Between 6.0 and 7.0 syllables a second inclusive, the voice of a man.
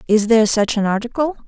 No: 6.5 syllables/s; female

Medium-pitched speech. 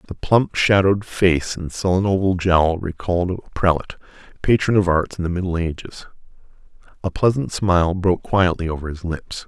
No: very low, 90 Hz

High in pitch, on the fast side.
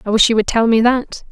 Yes: high, 225 Hz; fast, 320 wpm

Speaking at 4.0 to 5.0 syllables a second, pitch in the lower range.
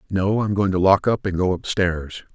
Yes: 4.9 syllables/s; very low, 95 Hz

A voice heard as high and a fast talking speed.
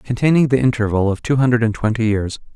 No: low, 115 Hz; fast, 210 wpm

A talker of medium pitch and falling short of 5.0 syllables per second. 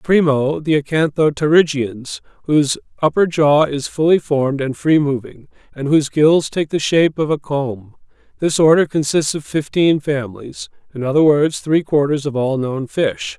Yes: medium, 145 Hz; 4.7 syllables/s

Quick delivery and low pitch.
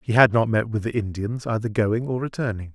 Yes: fast, 240 wpm; low, 110 Hz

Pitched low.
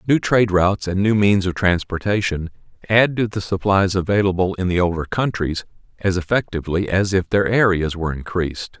Yes: very low, 95 Hz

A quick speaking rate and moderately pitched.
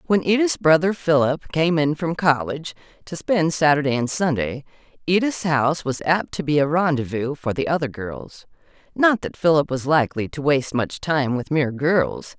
No: average, 180 wpm; medium, 150 Hz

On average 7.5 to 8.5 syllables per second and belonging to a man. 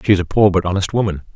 Yes: 7.8 syllables/s; male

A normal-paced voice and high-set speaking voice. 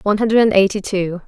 Yes: average, 190 wpm; high, 200 Hz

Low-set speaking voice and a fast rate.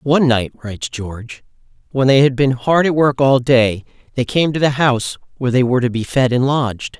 Yes: low, 130 Hz; fast, 225 wpm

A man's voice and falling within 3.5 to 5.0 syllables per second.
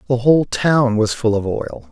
Yes: male; 4.7 syllables/s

